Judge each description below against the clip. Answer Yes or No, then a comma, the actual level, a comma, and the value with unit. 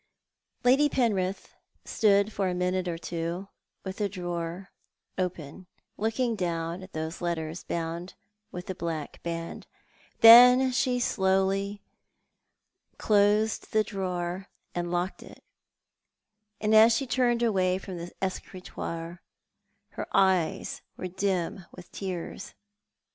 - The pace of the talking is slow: Yes, slow, 120 wpm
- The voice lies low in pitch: No, high, 190 Hz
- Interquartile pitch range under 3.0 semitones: No, average, 3.3 semitones